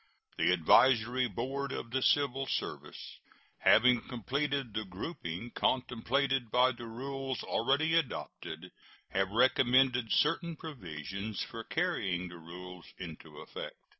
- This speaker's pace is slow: Yes, slow, 115 wpm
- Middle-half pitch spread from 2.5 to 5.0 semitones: No, wide, 5.6 semitones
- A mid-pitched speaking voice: No, low, 125 Hz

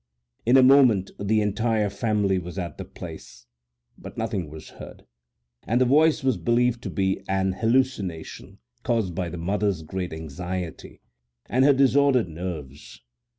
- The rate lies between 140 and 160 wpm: Yes, average, 150 wpm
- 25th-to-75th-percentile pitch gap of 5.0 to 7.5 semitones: Yes, wide, 5.5 semitones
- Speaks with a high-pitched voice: No, low, 100 Hz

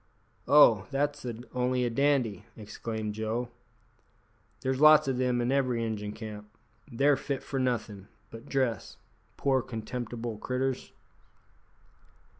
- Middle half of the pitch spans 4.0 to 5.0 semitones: No, average, 3.3 semitones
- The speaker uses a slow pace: Yes, slow, 115 wpm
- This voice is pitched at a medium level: No, low, 125 Hz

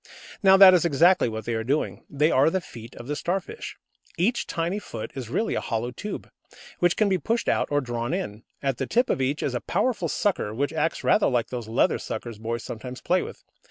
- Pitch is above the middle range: No, medium, 145 Hz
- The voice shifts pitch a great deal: Yes, wide, 7.7 semitones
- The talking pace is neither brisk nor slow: No, fast, 225 wpm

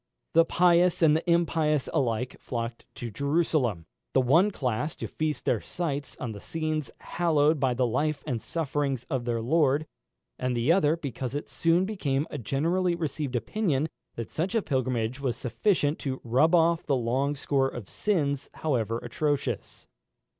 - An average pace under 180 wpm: Yes, average, 160 wpm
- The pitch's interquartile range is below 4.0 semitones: No, average, 4.5 semitones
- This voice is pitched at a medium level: Yes, medium, 145 Hz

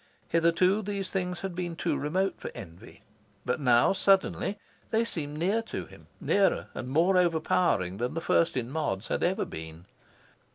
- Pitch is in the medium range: Yes, medium, 170 Hz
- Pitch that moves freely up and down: Yes, wide, 6.9 semitones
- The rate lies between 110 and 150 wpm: No, average, 165 wpm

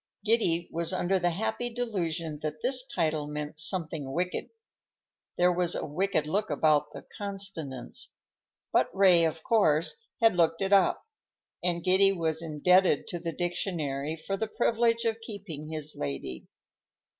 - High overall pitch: No, medium, 175 Hz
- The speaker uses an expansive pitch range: No, average, 4.1 semitones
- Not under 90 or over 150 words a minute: Yes, average, 140 wpm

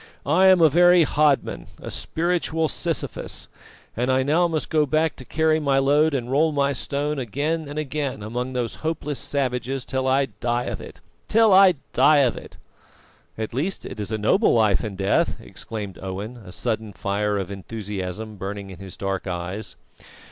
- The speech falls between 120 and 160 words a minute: No, average, 175 wpm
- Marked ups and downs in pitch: Yes, wide, 6.6 semitones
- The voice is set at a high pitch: No, low, 130 Hz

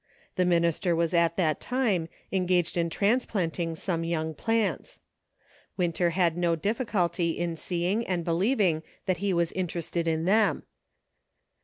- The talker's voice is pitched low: No, medium, 175 Hz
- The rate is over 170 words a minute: No, slow, 135 wpm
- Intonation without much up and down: Yes, narrow, 2.3 semitones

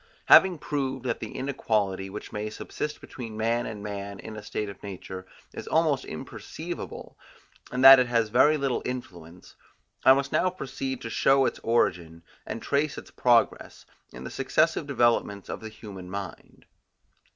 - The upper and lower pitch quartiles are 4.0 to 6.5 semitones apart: Yes, average, 4.8 semitones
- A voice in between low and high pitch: No, low, 115 Hz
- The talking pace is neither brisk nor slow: Yes, average, 160 wpm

